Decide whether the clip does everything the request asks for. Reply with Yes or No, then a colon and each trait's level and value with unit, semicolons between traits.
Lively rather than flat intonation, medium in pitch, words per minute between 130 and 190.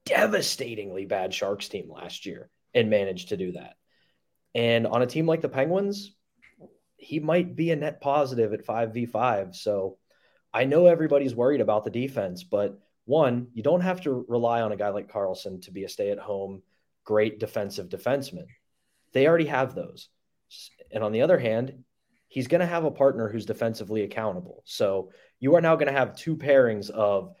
No: wide, 6.4 semitones; low, 125 Hz; average, 180 wpm